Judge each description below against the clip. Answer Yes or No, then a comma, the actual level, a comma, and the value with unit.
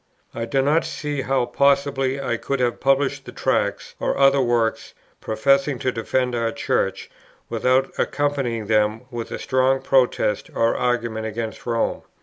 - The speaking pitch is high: No, low, 130 Hz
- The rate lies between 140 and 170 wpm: Yes, average, 150 wpm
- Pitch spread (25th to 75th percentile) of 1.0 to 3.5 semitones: Yes, average, 2.9 semitones